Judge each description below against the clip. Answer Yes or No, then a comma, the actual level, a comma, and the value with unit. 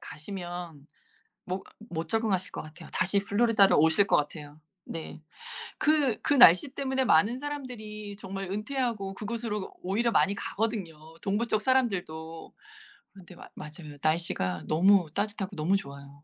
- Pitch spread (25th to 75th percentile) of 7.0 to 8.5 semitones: No, wide, 5.4 semitones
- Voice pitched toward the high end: Yes, high, 195 Hz